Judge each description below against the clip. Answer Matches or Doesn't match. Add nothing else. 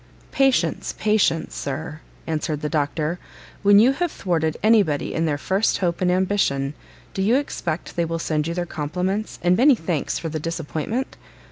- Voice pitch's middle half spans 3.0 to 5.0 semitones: Matches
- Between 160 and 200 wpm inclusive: Matches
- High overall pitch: Doesn't match